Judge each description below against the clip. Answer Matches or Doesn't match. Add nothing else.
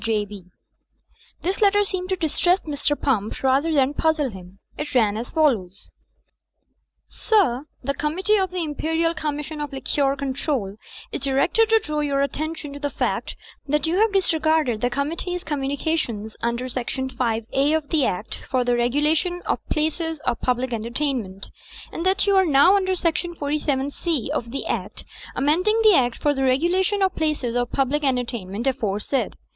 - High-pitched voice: Matches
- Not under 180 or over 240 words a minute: Doesn't match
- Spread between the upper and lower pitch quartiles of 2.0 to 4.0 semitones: Doesn't match